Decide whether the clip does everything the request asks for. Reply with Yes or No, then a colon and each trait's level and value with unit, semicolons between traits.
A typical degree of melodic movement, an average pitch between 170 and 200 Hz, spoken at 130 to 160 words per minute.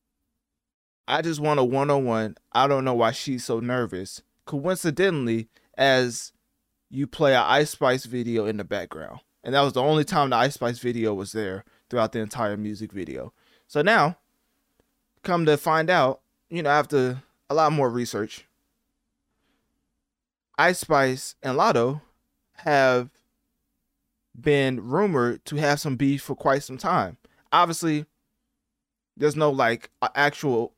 No: average, 4.2 semitones; low, 135 Hz; average, 140 wpm